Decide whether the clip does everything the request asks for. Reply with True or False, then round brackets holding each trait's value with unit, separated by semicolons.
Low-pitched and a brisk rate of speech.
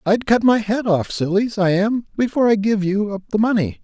False (210 Hz; 235 wpm)